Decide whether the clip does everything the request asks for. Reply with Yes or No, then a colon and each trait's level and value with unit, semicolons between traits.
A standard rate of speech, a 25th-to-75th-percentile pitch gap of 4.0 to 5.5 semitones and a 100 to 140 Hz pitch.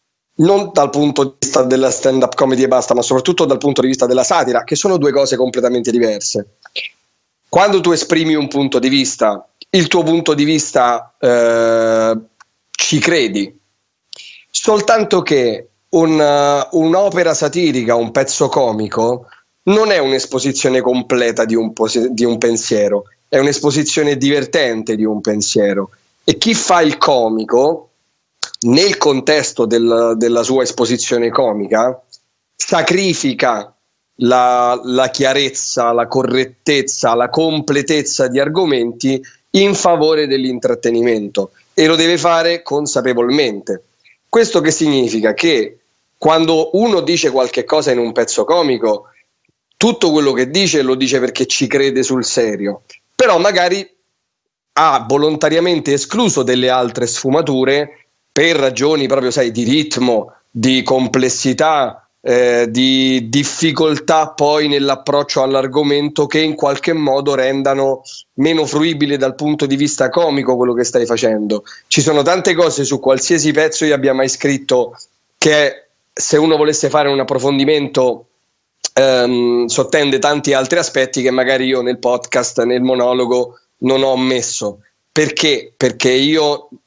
No: average, 135 wpm; average, 3.6 semitones; low, 135 Hz